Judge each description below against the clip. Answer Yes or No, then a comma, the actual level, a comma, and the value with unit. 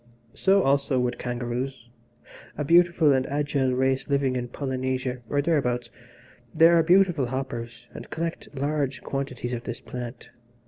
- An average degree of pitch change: Yes, average, 3.0 semitones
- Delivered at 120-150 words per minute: Yes, average, 140 wpm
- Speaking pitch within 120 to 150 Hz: Yes, low, 135 Hz